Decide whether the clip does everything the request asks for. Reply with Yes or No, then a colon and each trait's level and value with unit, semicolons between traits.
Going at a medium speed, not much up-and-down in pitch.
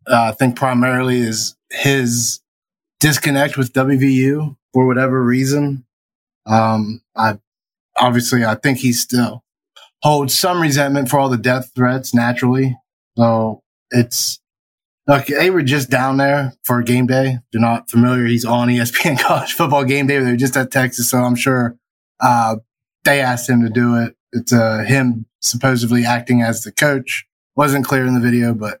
Yes: average, 160 wpm; narrow, 2.3 semitones